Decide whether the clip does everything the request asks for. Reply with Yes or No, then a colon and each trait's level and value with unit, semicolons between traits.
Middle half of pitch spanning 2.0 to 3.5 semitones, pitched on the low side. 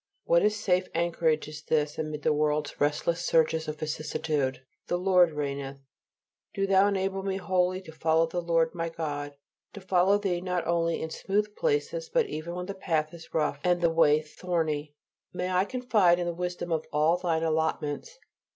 No: average, 3.1 semitones; medium, 170 Hz